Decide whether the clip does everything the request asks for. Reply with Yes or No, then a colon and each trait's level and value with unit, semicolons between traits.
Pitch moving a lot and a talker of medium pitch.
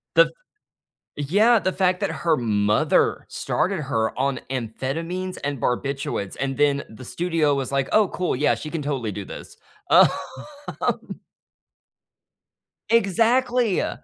Yes: wide, 6.0 semitones; medium, 145 Hz